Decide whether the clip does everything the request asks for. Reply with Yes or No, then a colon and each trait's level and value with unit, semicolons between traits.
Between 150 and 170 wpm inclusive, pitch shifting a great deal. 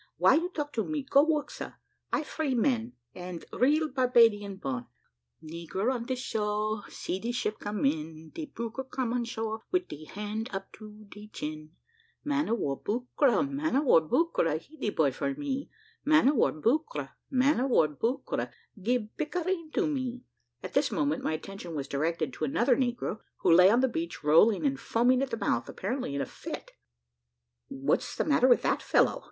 No: average, 190 wpm; wide, 6.8 semitones